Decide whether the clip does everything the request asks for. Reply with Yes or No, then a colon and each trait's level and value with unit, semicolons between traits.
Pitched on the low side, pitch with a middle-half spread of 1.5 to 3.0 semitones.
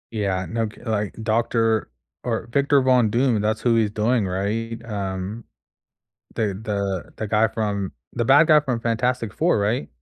Yes: low, 110 Hz; narrow, 2.4 semitones